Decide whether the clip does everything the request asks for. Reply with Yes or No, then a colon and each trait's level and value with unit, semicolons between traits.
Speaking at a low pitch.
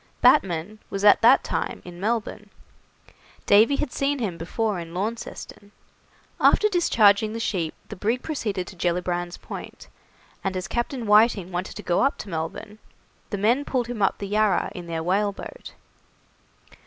No: high, 205 Hz